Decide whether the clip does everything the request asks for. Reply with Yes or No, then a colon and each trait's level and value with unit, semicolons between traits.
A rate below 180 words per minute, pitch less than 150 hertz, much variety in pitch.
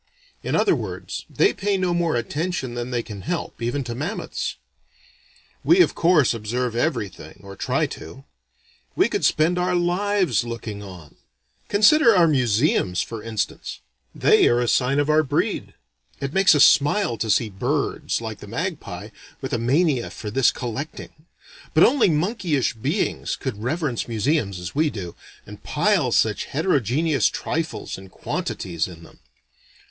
Yes: average, 155 wpm; low, 135 Hz; wide, 6.6 semitones